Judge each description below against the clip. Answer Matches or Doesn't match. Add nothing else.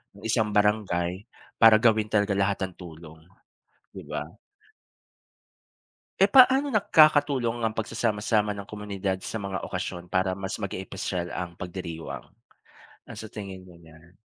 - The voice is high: Doesn't match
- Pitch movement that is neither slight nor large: Matches